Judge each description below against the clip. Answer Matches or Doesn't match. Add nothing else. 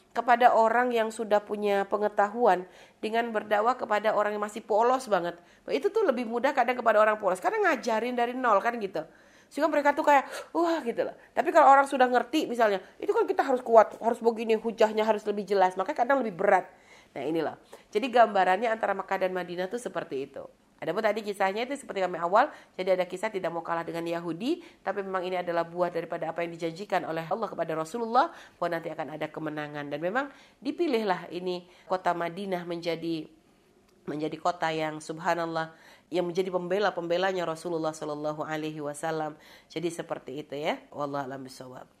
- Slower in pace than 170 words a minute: Doesn't match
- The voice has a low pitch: Doesn't match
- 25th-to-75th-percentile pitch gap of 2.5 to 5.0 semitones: Doesn't match